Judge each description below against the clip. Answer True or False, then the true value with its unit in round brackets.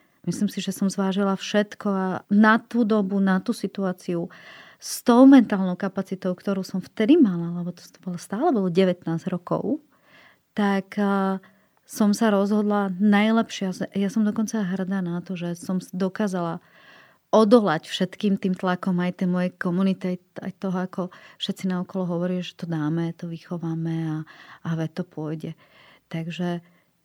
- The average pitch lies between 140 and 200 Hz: True (190 Hz)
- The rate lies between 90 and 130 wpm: False (150 wpm)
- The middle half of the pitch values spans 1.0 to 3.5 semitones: True (2.5 semitones)